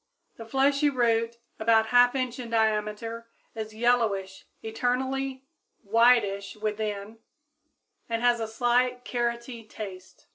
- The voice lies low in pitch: No, high, 230 Hz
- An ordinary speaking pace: No, slow, 115 wpm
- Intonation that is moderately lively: No, narrow, 2.2 semitones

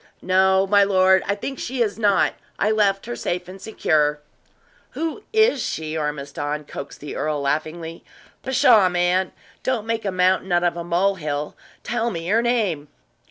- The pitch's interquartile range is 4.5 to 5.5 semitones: Yes, average, 4.9 semitones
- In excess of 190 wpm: No, average, 165 wpm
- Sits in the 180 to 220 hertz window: Yes, medium, 185 Hz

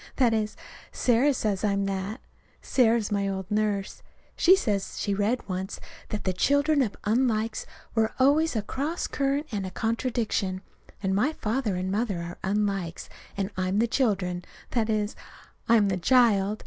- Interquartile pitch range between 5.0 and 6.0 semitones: No, average, 3.8 semitones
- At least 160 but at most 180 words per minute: Yes, average, 165 wpm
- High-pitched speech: Yes, high, 215 Hz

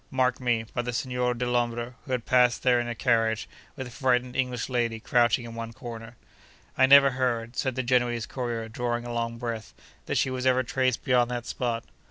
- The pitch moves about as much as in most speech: No, narrow, 1.4 semitones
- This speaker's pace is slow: No, fast, 205 wpm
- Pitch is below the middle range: Yes, low, 120 Hz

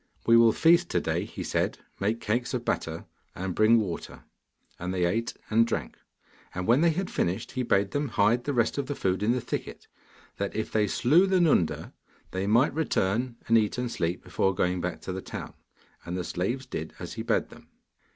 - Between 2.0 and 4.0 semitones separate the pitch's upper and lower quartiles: No, average, 5.2 semitones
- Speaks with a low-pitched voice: Yes, low, 110 Hz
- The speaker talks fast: Yes, fast, 210 wpm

